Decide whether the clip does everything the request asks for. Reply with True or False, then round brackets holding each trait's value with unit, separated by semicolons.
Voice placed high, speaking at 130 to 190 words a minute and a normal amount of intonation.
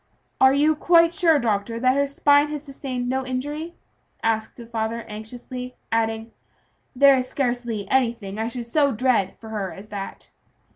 True (250 Hz; 160 wpm; 3.9 semitones)